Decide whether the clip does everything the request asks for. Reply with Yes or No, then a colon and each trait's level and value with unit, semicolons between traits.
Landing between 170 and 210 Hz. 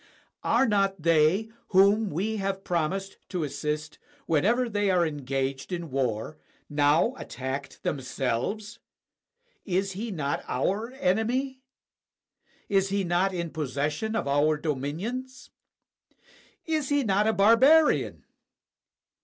Yes: medium, 185 Hz